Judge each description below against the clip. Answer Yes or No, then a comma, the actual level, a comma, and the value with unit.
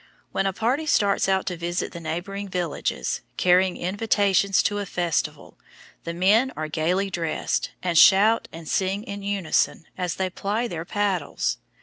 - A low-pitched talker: No, high, 190 Hz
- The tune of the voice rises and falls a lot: No, average, 2.7 semitones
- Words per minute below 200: Yes, average, 155 wpm